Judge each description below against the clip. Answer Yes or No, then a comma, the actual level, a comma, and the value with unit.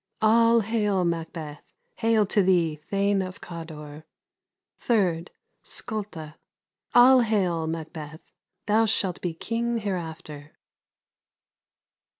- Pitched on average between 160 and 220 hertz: Yes, medium, 185 Hz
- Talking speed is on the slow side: Yes, slow, 100 wpm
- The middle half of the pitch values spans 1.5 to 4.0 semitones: No, average, 5.1 semitones